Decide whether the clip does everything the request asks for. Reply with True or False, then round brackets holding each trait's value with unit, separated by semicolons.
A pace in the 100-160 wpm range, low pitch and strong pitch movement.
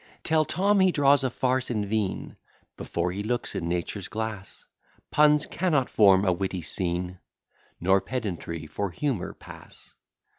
True (145 wpm; 105 Hz; 7.2 semitones)